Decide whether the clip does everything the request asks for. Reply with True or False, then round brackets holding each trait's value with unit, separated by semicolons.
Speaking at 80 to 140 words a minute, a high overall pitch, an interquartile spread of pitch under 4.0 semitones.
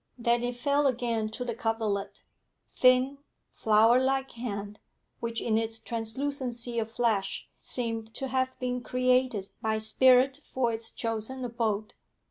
True (135 wpm; 235 Hz; 2.4 semitones)